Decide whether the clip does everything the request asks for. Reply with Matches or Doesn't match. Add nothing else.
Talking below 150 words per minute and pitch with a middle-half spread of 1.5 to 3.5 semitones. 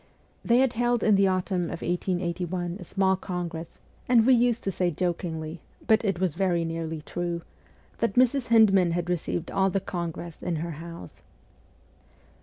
Doesn't match